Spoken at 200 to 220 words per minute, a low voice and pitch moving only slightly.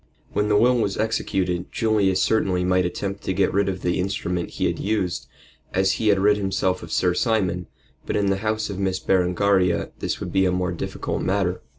Yes: fast, 205 wpm; very low, 95 Hz; narrow, 2.1 semitones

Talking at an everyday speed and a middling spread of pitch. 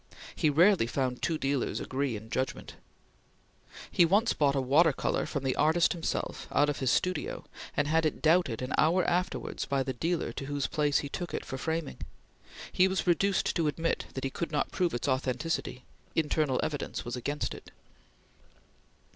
Yes: average, 180 wpm; average, 4.0 semitones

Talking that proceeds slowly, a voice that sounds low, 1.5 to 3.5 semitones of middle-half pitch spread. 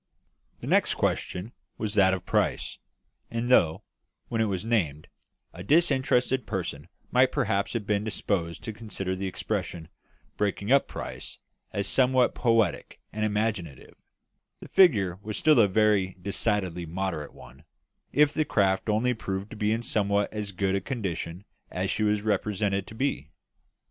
No: average, 150 wpm; low, 105 Hz; average, 3.1 semitones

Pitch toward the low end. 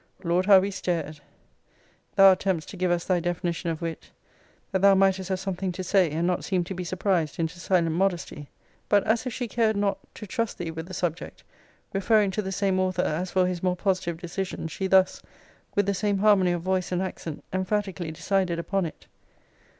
No: medium, 185 Hz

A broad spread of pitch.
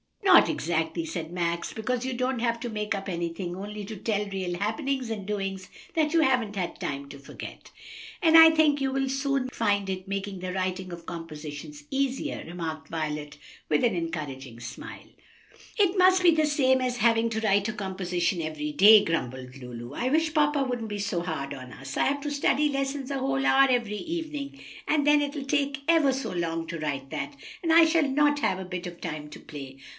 Yes: wide, 8.4 semitones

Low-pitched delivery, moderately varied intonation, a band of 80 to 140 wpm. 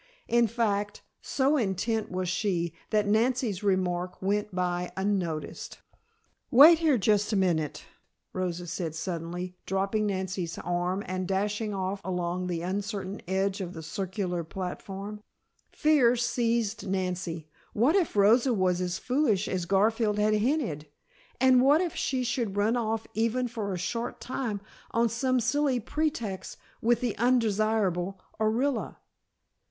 No: high, 205 Hz; average, 4.2 semitones; slow, 135 wpm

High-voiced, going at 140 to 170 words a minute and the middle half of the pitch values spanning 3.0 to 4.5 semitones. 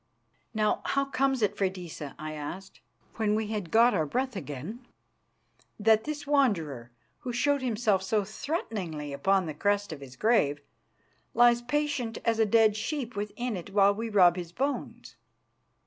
No: high, 210 Hz; average, 155 wpm; average, 5.2 semitones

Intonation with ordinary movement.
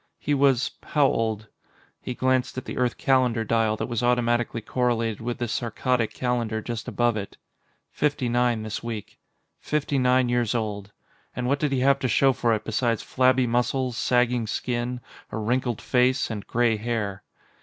No: narrow, 2.1 semitones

